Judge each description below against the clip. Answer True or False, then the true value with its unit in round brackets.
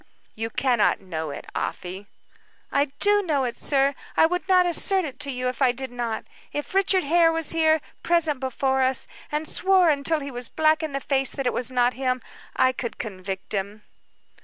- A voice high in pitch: True (270 Hz)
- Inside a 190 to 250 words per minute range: True (195 wpm)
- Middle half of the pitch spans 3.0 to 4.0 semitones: False (4.5 semitones)